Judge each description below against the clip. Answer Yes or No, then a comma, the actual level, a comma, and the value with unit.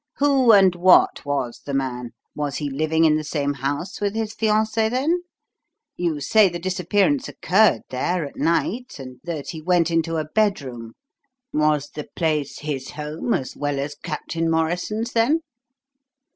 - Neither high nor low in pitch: Yes, medium, 165 Hz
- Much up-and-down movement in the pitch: Yes, wide, 6.1 semitones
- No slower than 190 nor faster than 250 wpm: No, average, 160 wpm